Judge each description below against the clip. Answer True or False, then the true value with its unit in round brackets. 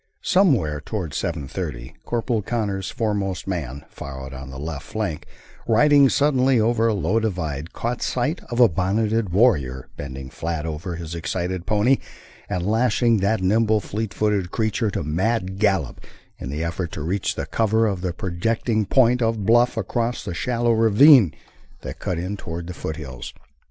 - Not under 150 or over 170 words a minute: True (165 wpm)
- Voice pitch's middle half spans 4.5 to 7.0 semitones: True (5.4 semitones)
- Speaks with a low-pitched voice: True (100 Hz)